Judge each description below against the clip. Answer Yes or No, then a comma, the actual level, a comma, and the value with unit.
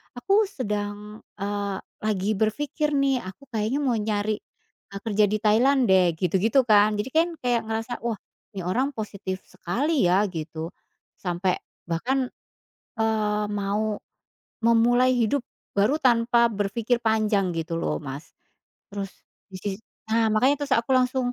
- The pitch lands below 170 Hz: No, high, 215 Hz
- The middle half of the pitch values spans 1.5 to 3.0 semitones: No, average, 3.7 semitones